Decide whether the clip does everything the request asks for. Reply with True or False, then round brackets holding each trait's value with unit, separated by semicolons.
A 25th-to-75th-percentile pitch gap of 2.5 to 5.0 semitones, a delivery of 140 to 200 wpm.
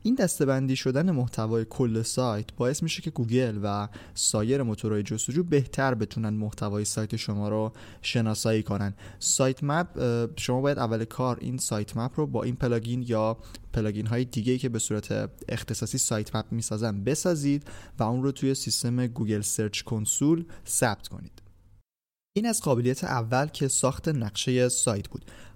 True (3.6 semitones; 155 wpm)